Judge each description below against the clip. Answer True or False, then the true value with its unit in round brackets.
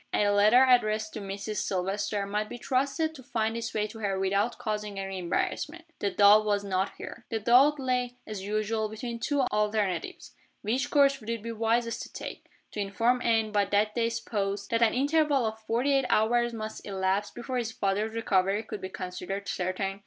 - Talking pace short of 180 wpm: False (190 wpm)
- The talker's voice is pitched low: False (215 Hz)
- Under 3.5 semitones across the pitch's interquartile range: True (2.9 semitones)